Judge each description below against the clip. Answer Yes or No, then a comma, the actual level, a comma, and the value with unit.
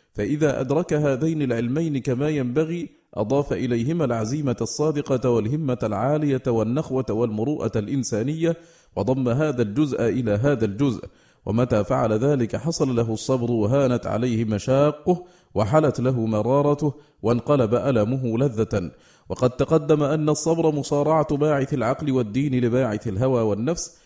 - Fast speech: No, average, 115 wpm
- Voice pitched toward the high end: No, low, 130 Hz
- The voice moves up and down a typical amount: Yes, average, 4.4 semitones